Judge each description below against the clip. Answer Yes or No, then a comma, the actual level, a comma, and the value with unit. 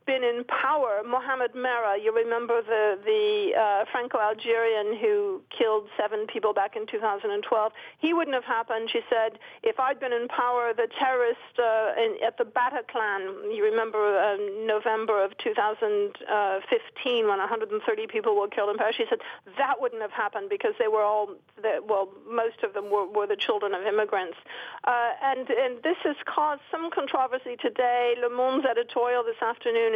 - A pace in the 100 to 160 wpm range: No, average, 170 wpm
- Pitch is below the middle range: No, high, 240 Hz